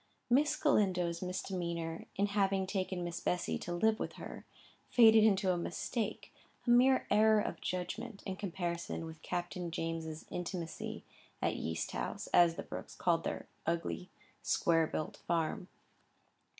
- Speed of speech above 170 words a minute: No, average, 140 wpm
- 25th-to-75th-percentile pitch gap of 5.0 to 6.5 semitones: No, average, 3.3 semitones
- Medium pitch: Yes, medium, 180 Hz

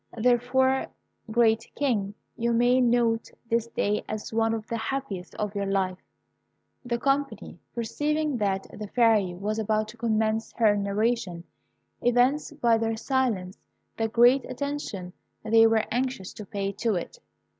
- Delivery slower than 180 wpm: Yes, average, 145 wpm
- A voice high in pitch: Yes, high, 225 Hz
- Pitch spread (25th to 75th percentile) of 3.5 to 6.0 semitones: No, average, 2.7 semitones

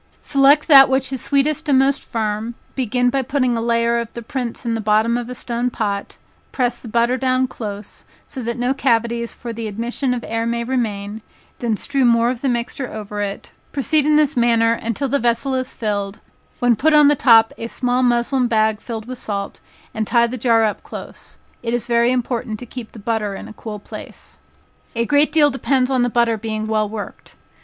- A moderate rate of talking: No, fast, 210 wpm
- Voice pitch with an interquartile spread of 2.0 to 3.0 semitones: Yes, narrow, 2.5 semitones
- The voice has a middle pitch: No, high, 235 Hz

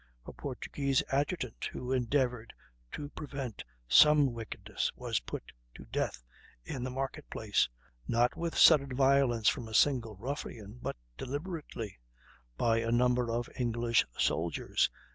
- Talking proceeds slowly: Yes, slow, 130 wpm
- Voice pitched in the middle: No, low, 125 Hz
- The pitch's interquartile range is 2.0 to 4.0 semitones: Yes, average, 3.2 semitones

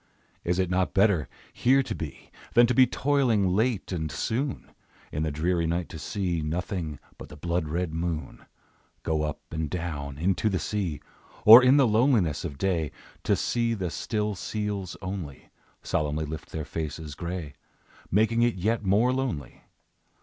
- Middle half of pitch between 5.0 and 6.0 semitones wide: Yes, wide, 5.6 semitones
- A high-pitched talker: No, very low, 90 Hz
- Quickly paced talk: No, average, 165 wpm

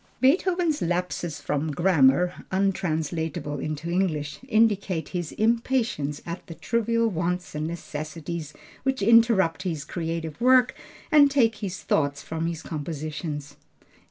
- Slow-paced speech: Yes, slow, 120 wpm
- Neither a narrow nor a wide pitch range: No, wide, 6.3 semitones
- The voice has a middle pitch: Yes, medium, 170 Hz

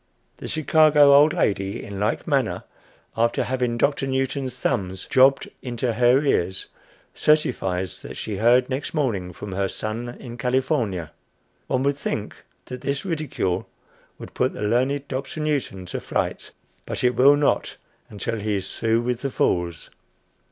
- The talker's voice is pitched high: No, low, 125 Hz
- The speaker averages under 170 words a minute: Yes, average, 155 wpm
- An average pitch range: Yes, average, 5.0 semitones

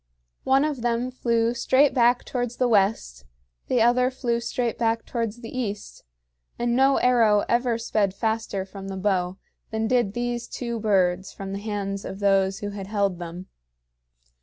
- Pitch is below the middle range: No, high, 225 Hz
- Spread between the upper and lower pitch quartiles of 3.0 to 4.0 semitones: Yes, average, 3.5 semitones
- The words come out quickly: No, average, 165 wpm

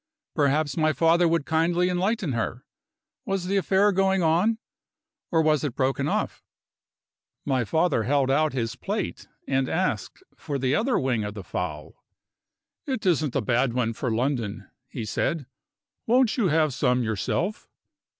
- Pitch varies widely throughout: Yes, wide, 6.1 semitones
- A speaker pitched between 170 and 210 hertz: No, medium, 150 Hz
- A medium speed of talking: Yes, average, 150 wpm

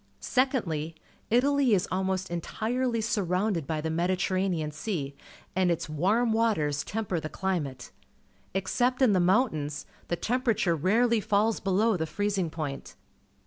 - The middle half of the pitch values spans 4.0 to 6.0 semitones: Yes, wide, 5.6 semitones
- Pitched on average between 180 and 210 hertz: Yes, high, 190 Hz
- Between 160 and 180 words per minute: No, slow, 135 wpm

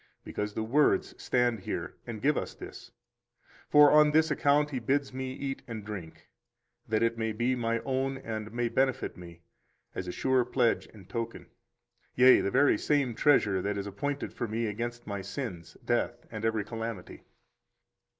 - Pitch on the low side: Yes, low, 115 Hz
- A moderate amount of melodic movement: Yes, average, 3.9 semitones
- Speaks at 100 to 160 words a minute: No, average, 170 wpm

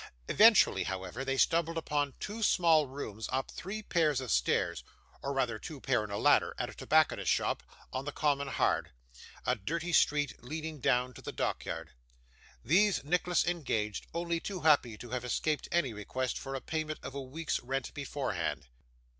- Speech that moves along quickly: No, average, 170 wpm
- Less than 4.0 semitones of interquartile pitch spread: No, average, 4.6 semitones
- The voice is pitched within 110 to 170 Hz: Yes, medium, 140 Hz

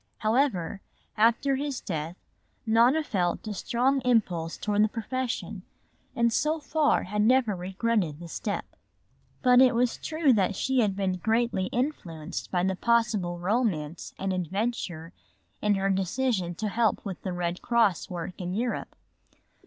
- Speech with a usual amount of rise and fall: Yes, average, 4.9 semitones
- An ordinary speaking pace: Yes, average, 150 wpm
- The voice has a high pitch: Yes, high, 210 Hz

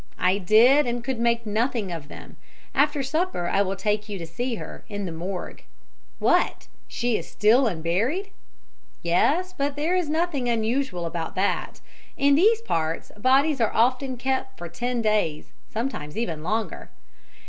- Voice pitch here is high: Yes, high, 235 Hz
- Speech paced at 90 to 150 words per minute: No, average, 160 wpm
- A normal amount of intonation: No, wide, 6.1 semitones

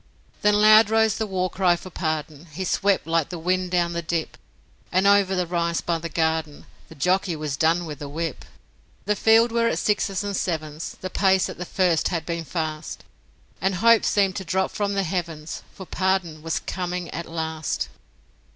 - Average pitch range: Yes, average, 3.0 semitones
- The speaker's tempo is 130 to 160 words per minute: No, average, 190 wpm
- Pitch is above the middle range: No, medium, 180 Hz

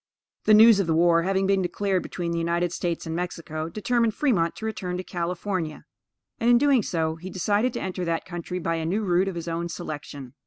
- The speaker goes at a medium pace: No, fast, 210 wpm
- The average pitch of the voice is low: No, medium, 180 Hz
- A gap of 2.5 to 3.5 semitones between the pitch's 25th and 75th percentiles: Yes, average, 3.1 semitones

